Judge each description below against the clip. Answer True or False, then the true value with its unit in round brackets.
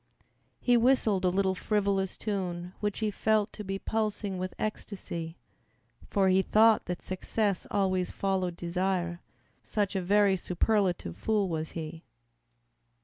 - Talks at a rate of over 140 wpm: False (135 wpm)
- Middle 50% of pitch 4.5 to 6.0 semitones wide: False (2.7 semitones)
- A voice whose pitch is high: True (195 Hz)